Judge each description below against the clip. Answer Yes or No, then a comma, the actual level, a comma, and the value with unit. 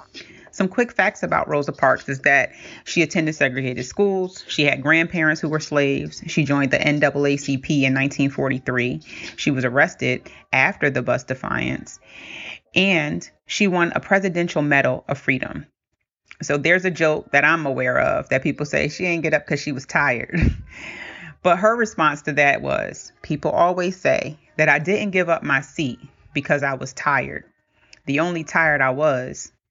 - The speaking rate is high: No, average, 170 wpm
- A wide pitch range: No, average, 3.8 semitones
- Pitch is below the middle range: No, medium, 150 Hz